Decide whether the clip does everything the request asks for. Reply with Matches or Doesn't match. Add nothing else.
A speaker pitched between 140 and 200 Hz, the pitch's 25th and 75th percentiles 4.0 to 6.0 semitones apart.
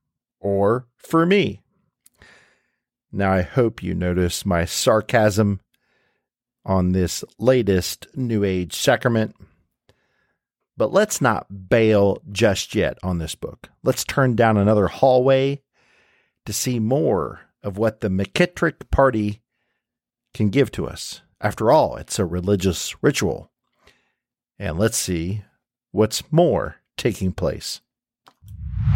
Doesn't match